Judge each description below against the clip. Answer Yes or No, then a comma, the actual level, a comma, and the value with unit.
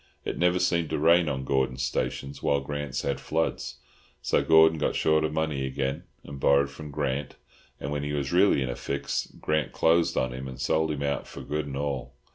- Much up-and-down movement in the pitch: No, narrow, 2.6 semitones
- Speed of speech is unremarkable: No, fast, 210 wpm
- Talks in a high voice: No, very low, 70 Hz